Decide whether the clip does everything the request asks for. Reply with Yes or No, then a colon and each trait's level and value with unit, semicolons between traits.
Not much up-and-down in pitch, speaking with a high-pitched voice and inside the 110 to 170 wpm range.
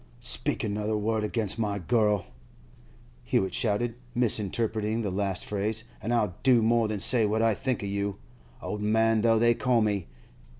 No: narrow, 1.9 semitones; low, 110 Hz; average, 160 wpm